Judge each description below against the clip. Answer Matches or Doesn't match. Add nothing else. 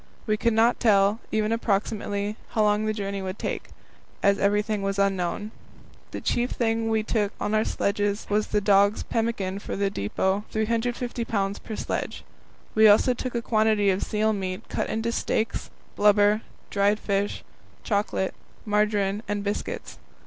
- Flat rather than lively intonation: Matches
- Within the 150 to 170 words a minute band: Matches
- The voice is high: Matches